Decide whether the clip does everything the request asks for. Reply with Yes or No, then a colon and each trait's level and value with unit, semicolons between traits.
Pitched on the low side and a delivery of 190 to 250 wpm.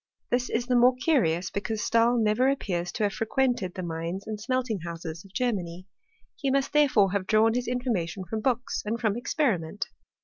No: high, 220 Hz; average, 195 wpm